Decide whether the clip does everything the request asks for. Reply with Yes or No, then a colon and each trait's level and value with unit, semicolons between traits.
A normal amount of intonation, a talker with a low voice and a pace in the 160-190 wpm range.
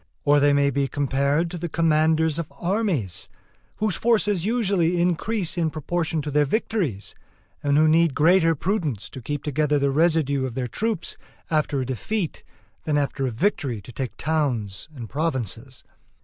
No: average, 4.0 semitones; medium, 155 Hz; average, 165 wpm